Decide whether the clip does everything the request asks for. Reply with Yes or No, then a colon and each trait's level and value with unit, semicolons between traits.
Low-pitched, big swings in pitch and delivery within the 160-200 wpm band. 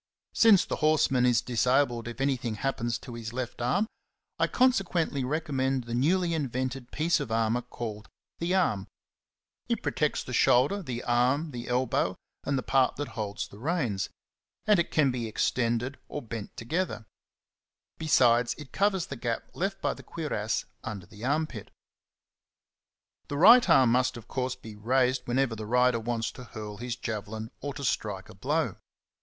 No: low, 125 Hz; average, 4.0 semitones; average, 170 wpm